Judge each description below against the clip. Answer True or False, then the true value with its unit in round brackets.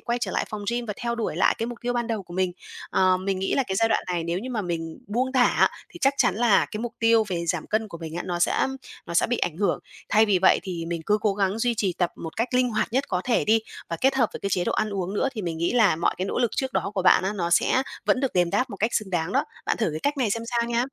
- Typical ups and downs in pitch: True (4.8 semitones)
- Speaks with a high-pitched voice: True (210 Hz)